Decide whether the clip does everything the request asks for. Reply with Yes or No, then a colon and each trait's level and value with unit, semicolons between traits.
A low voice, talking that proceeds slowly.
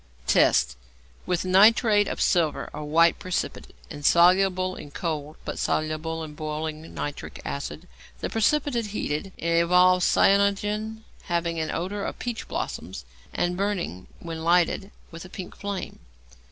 No: medium, 175 Hz; slow, 130 wpm